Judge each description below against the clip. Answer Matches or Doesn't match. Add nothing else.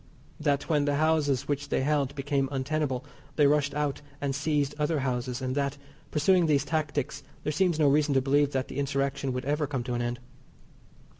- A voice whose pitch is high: Doesn't match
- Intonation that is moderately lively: Doesn't match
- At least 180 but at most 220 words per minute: Matches